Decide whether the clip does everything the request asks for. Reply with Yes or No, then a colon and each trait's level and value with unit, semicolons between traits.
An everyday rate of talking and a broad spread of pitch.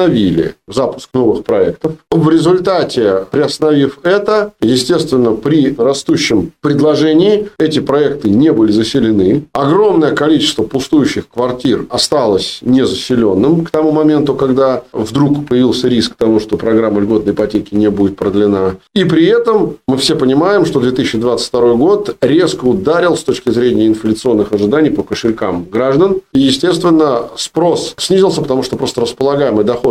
Yes: average, 130 wpm; wide, 5.9 semitones